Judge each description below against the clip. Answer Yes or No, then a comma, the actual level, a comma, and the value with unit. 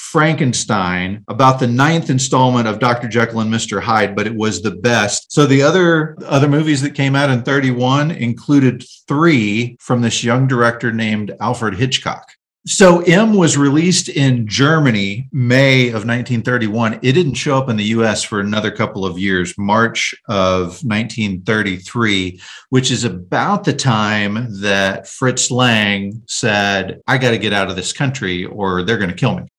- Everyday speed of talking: Yes, average, 165 wpm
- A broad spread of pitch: No, average, 4.3 semitones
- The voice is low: Yes, low, 120 Hz